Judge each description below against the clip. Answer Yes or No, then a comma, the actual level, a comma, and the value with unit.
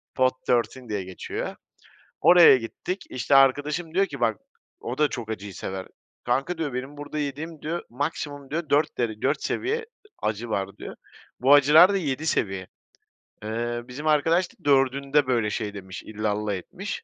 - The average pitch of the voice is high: No, low, 135 Hz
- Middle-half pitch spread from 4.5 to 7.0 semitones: Yes, average, 5.2 semitones